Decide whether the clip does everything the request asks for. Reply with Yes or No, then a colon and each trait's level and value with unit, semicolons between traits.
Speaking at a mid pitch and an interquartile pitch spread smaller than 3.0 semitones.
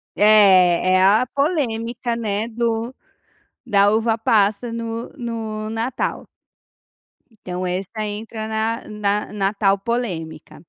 No: high, 220 Hz; narrow, 2.5 semitones